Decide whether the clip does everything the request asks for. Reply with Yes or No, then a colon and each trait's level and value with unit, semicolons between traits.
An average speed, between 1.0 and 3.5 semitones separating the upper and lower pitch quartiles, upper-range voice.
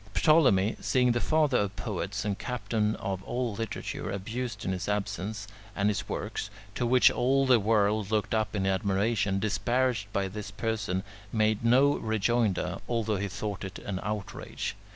No: average, 160 wpm; average, 3.1 semitones; low, 105 Hz